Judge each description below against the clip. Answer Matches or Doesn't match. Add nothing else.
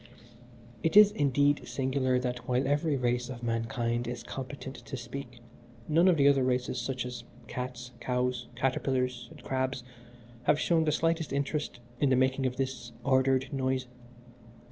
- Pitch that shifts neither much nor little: Doesn't match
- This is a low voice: Matches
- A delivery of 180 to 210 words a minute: Doesn't match